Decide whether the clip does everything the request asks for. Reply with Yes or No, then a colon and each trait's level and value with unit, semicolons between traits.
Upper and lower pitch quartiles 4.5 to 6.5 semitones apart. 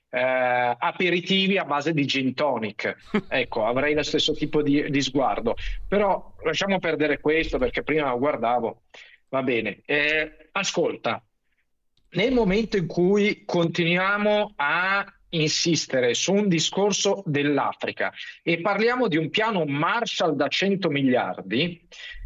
Yes: average, 5.2 semitones